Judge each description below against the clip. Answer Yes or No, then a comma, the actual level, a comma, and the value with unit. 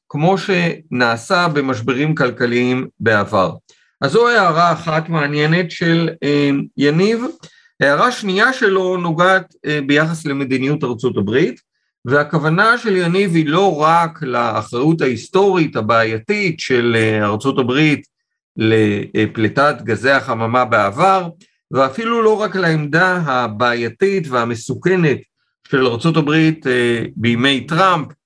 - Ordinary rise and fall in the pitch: No, wide, 6.3 semitones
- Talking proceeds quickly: No, slow, 100 wpm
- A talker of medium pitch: Yes, medium, 150 Hz